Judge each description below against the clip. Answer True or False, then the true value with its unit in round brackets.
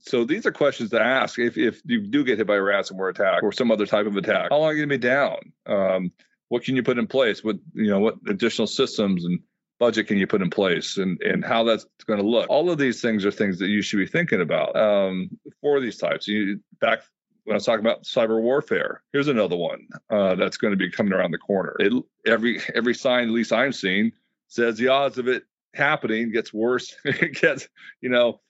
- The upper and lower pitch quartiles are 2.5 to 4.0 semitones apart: True (3.6 semitones)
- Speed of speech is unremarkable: False (240 wpm)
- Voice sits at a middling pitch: False (115 Hz)